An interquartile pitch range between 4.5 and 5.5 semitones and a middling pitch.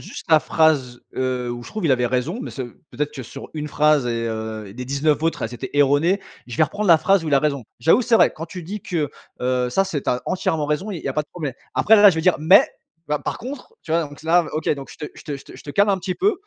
Yes: average, 5.2 semitones; medium, 150 Hz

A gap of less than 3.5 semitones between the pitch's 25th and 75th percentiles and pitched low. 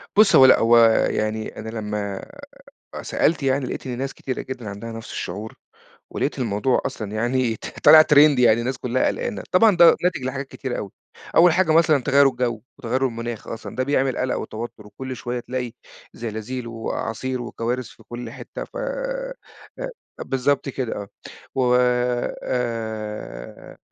Yes: average, 3.0 semitones; low, 125 Hz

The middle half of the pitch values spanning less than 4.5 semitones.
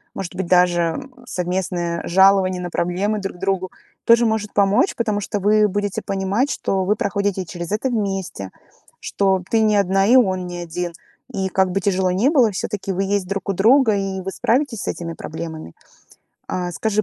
Yes: narrow, 2.6 semitones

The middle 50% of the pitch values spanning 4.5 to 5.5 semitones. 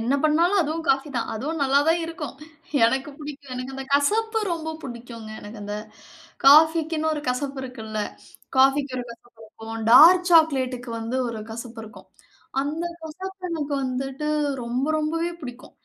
Yes: average, 4.8 semitones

